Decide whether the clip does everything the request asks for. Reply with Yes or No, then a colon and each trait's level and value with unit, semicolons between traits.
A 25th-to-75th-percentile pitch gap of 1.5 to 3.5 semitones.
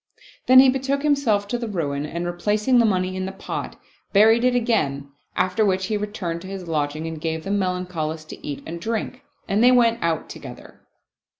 No: wide, 5.5 semitones